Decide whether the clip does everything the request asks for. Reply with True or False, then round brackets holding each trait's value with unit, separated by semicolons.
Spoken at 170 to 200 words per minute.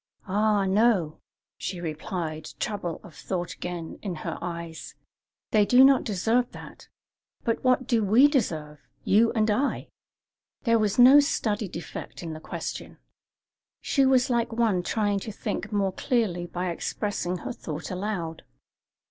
False (145 wpm)